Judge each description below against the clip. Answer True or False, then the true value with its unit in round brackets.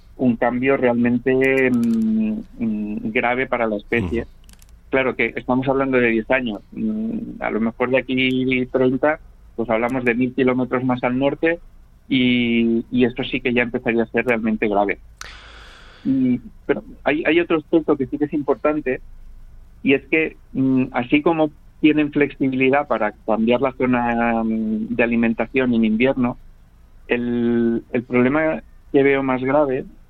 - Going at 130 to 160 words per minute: True (150 wpm)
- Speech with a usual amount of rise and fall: True (3.5 semitones)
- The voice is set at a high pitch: False (130 Hz)